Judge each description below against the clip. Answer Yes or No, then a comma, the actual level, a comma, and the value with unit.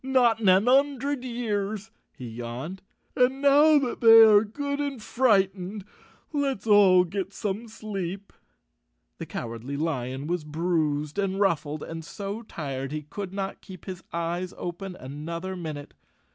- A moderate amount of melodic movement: No, wide, 5.7 semitones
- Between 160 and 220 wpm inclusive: No, average, 150 wpm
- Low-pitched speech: No, high, 195 Hz